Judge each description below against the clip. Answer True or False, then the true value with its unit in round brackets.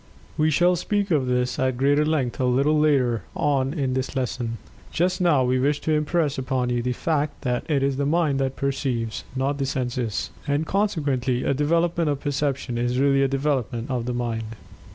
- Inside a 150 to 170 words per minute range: False (195 wpm)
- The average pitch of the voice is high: False (135 Hz)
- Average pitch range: True (3.1 semitones)